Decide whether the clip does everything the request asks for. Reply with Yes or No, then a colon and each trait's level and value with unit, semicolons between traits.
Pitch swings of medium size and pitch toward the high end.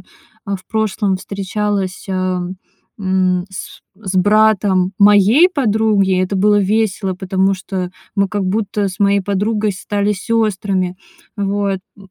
No: narrow, 1.9 semitones; high, 200 Hz